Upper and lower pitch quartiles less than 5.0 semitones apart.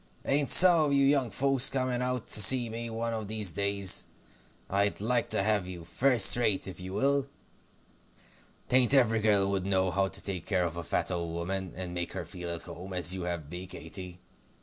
No: average, 5.3 semitones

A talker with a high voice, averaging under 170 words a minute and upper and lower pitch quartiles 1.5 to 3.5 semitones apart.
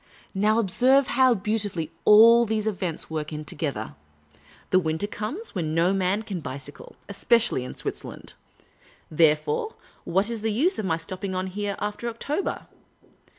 No: high, 200 Hz; average, 150 wpm; wide, 5.4 semitones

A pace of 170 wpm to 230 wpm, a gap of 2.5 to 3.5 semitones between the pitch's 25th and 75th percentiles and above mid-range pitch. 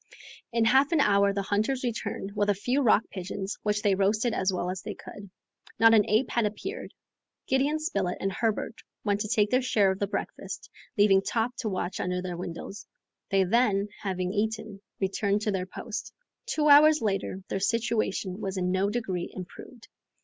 Yes: average, 185 wpm; average, 3.0 semitones; high, 205 Hz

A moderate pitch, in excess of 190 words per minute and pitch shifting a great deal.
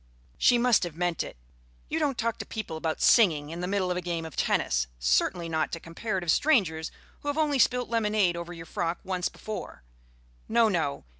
Yes: medium, 180 Hz; average, 200 wpm; wide, 5.7 semitones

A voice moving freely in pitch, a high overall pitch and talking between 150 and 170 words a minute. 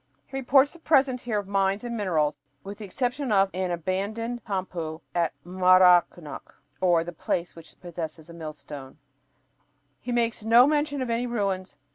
Yes: wide, 5.7 semitones; high, 195 Hz; average, 160 wpm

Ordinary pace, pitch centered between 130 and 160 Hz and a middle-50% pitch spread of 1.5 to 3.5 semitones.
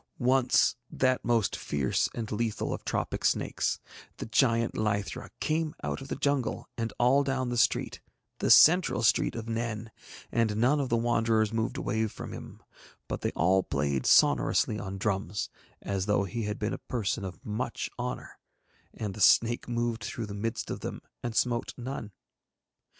No: average, 170 wpm; low, 115 Hz; average, 2.7 semitones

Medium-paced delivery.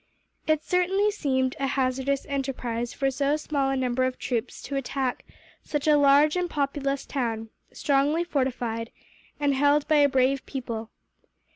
Yes: average, 150 wpm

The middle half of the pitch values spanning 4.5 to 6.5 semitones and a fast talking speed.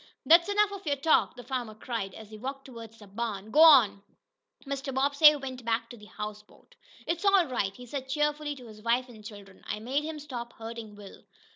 Yes: average, 4.9 semitones; fast, 210 wpm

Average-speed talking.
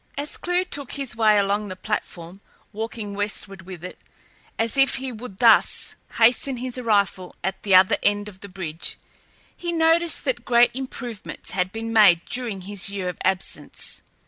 Yes: average, 170 wpm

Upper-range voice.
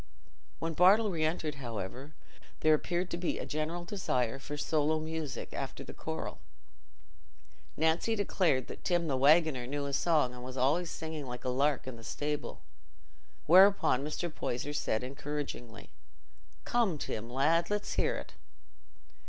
No: medium, 150 Hz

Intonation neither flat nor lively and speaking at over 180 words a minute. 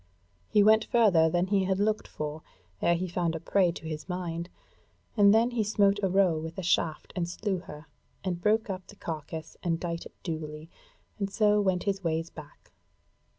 Yes: average, 3.6 semitones; average, 195 wpm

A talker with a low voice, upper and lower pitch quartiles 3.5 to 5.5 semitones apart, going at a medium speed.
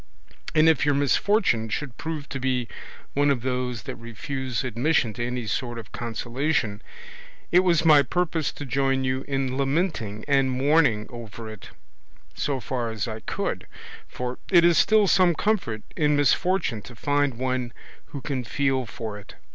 Yes: low, 130 Hz; average, 3.9 semitones; average, 165 wpm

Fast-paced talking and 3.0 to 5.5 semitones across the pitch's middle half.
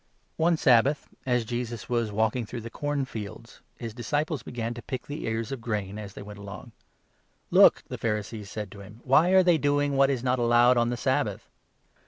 Yes: fast, 225 wpm; average, 3.9 semitones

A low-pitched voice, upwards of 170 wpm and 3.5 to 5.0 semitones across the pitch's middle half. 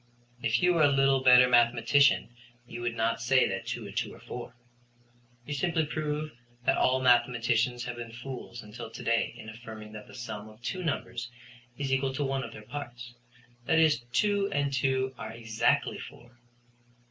No: low, 125 Hz; average, 180 wpm; average, 3.1 semitones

